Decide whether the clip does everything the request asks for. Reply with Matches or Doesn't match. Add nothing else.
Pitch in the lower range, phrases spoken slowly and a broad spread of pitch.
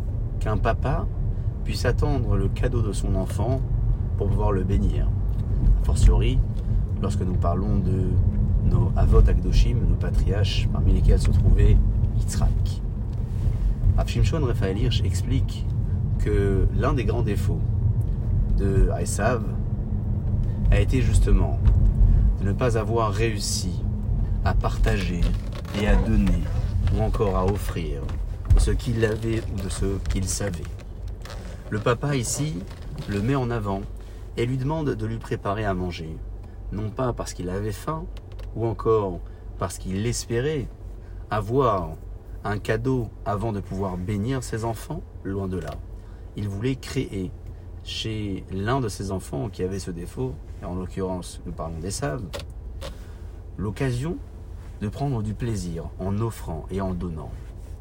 Doesn't match